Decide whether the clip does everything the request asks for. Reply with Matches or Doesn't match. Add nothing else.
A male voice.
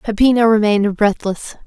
Doesn't match